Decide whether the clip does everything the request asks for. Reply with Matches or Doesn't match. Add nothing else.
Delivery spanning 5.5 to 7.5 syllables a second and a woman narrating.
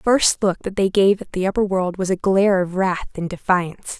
Matches